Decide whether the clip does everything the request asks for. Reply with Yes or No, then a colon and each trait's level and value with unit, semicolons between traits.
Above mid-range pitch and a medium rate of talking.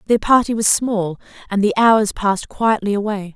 Yes: high, 210 Hz; average, 180 wpm